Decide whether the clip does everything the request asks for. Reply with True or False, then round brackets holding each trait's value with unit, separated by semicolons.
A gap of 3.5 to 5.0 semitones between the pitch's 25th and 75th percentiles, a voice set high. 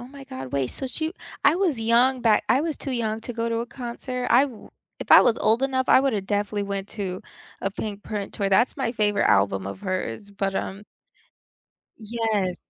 True (4.2 semitones; 225 Hz)